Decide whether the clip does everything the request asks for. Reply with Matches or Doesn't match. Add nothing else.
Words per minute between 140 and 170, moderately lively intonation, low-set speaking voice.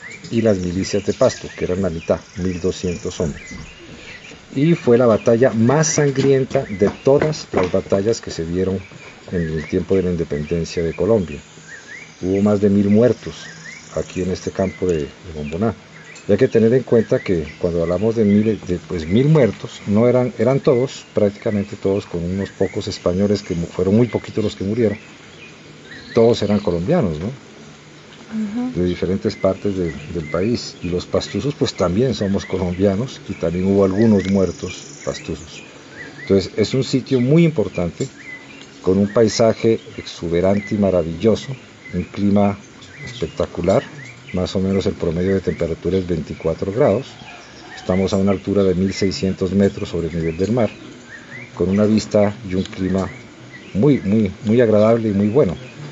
Matches